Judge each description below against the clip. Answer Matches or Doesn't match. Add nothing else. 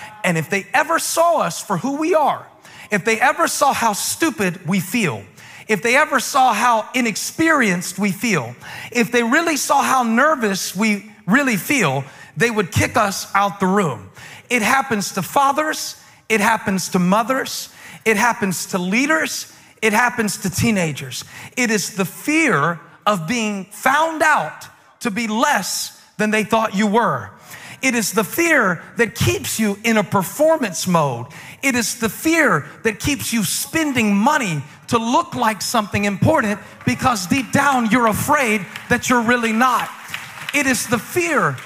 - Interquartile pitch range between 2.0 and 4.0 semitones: Doesn't match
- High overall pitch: Matches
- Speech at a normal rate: Matches